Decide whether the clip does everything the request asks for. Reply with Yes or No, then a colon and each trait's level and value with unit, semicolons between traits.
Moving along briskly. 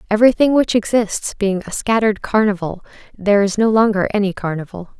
No: average, 155 wpm